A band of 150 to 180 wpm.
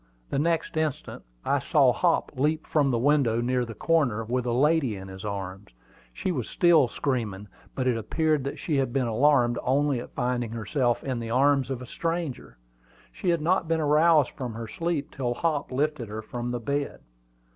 No: average, 190 wpm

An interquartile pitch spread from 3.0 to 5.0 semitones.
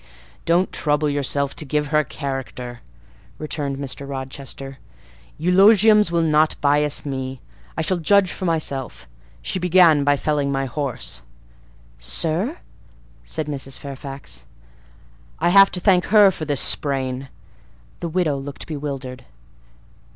Yes: average, 3.8 semitones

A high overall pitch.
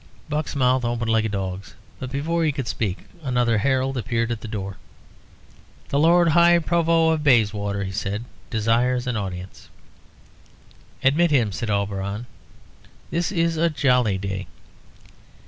No: low, 120 Hz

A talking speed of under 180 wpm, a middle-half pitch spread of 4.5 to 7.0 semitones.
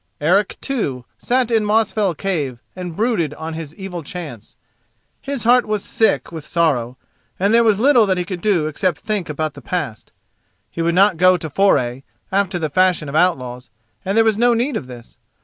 No: average, 190 wpm; wide, 5.5 semitones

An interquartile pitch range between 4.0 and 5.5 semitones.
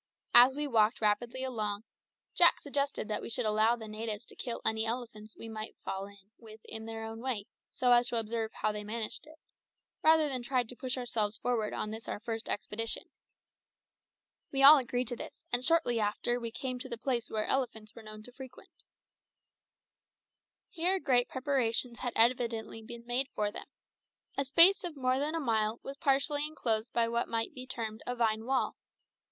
No: average, 2.8 semitones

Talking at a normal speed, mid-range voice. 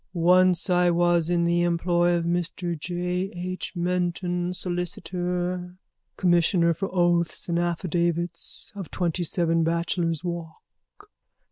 No: slow, 115 wpm; medium, 175 Hz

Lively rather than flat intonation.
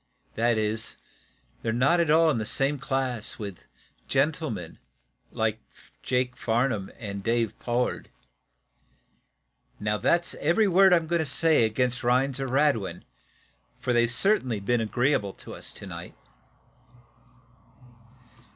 No: average, 4.9 semitones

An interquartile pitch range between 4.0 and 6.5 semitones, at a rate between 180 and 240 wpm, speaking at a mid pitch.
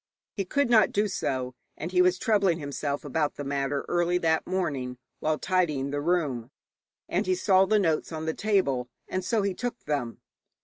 Yes: average, 5.0 semitones; average, 185 wpm; medium, 165 Hz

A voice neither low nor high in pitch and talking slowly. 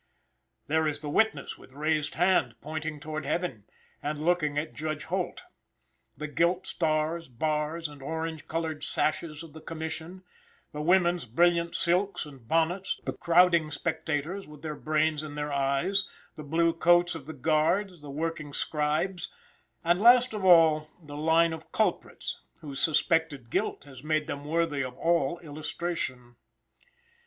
No: medium, 155 Hz; average, 150 wpm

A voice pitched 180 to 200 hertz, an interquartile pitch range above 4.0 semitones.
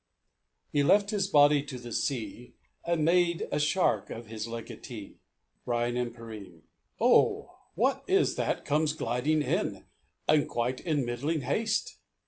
No: medium, 140 Hz; average, 4.7 semitones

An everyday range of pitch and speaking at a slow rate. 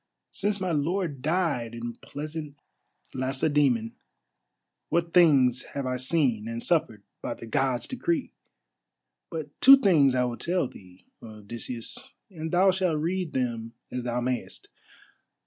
No: wide, 6.0 semitones; slow, 130 wpm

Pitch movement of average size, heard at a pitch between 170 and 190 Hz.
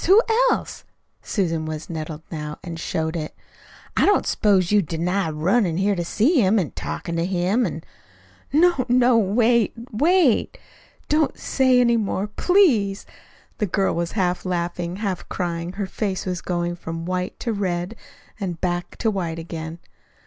Yes: average, 4.6 semitones; medium, 185 Hz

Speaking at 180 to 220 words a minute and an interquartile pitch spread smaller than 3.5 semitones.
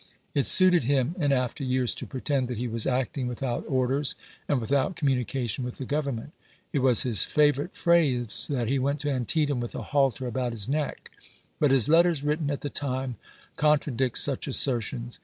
Yes: average, 190 wpm; average, 2.8 semitones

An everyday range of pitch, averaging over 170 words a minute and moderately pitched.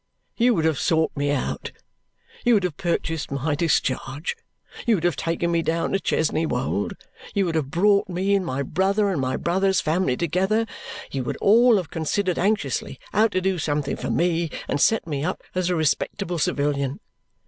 Yes: average, 4.7 semitones; average, 185 wpm; medium, 170 Hz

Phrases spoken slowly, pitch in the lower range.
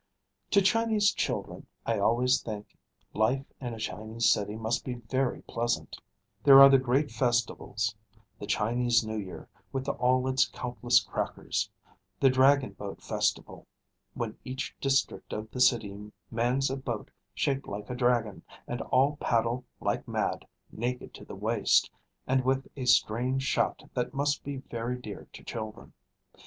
No: average, 150 wpm; low, 125 Hz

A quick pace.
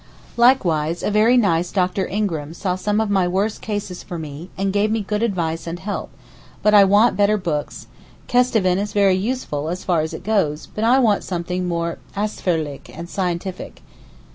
No: average, 175 wpm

